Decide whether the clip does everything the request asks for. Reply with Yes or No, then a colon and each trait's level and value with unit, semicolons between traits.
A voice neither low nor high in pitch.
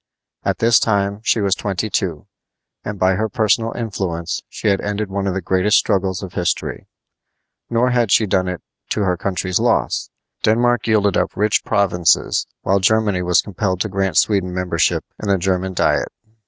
No: low, 100 Hz